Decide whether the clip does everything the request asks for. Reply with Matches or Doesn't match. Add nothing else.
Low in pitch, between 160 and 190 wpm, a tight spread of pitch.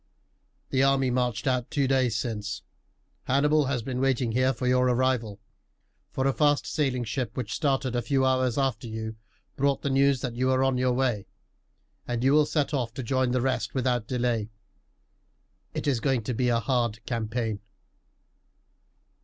Matches